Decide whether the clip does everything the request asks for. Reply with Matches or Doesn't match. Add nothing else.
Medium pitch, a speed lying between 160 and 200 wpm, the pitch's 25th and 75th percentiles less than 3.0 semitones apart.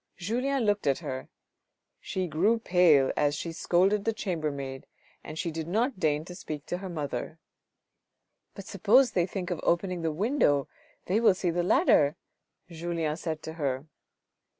Doesn't match